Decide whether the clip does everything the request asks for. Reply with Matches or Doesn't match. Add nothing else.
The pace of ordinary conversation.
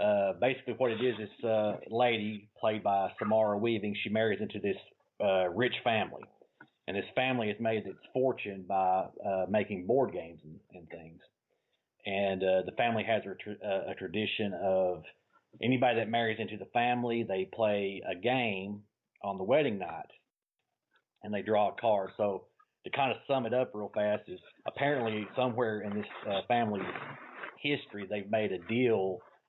Matches